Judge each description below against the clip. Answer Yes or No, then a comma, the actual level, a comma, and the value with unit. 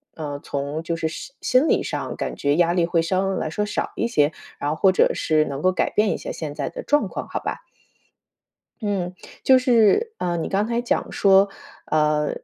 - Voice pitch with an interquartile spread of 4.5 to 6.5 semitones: Yes, average, 5.3 semitones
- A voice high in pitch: No, medium, 175 Hz